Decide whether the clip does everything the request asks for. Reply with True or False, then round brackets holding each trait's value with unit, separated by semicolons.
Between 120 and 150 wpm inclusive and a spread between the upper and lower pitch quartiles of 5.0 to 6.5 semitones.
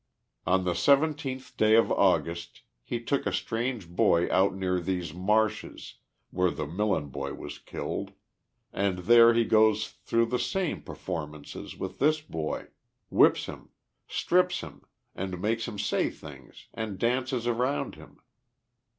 True (140 wpm; 5.3 semitones)